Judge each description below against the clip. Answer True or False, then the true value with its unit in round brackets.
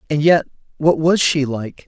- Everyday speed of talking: True (160 wpm)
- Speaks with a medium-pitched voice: True (150 Hz)